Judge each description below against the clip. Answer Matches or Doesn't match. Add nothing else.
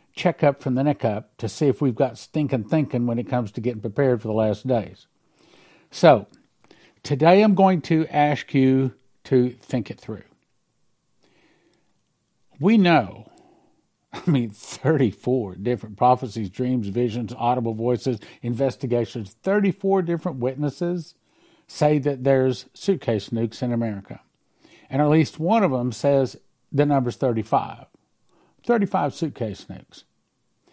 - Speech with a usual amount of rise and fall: Matches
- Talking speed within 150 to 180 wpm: Doesn't match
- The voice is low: Matches